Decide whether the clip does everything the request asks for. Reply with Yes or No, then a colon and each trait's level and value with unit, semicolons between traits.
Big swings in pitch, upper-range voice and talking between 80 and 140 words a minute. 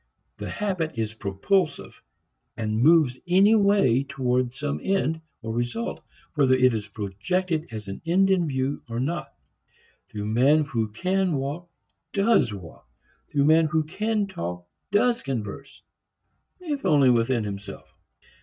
No: wide, 8.0 semitones; medium, 140 Hz; slow, 135 wpm